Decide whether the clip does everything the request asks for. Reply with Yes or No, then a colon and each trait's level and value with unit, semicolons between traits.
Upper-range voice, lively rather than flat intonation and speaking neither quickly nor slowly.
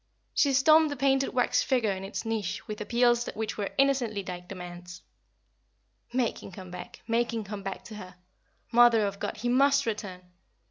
No: high, 225 Hz; average, 4.3 semitones; average, 180 wpm